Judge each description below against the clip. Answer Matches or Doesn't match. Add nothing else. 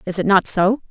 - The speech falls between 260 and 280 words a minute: Matches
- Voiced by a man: Doesn't match